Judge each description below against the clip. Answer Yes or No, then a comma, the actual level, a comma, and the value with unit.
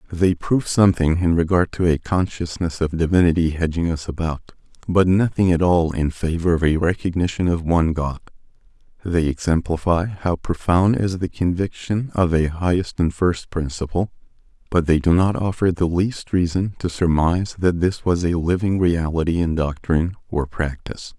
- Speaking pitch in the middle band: No, very low, 85 Hz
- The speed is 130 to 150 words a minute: No, average, 165 wpm